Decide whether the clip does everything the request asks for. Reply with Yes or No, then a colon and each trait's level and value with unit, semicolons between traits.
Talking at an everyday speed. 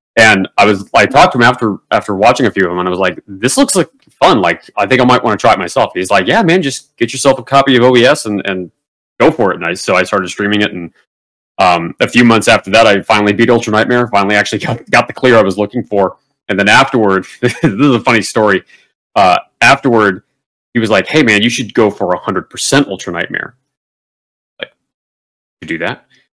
No: fast, 240 wpm